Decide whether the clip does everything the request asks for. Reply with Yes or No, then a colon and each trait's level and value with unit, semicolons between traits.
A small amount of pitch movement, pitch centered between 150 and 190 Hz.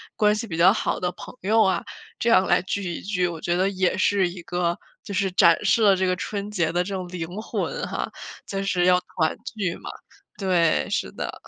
Yes: narrow, 2.2 semitones; medium, 185 Hz